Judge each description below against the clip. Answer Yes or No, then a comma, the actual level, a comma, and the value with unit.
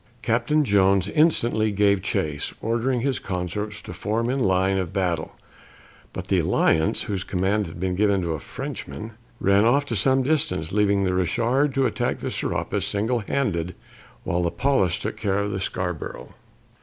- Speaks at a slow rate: No, average, 170 wpm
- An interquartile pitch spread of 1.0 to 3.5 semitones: No, average, 4.3 semitones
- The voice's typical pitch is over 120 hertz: No, low, 100 Hz